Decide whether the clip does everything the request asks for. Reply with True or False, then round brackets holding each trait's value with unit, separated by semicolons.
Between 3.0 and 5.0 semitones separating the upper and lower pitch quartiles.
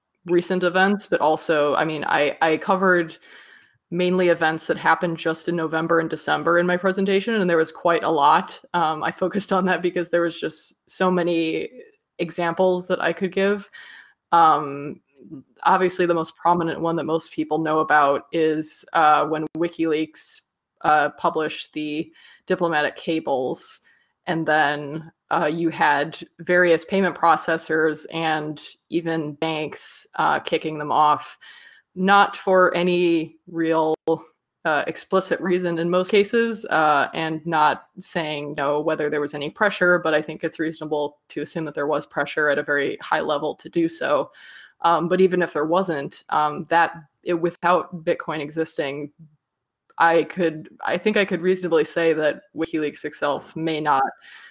False (2.4 semitones)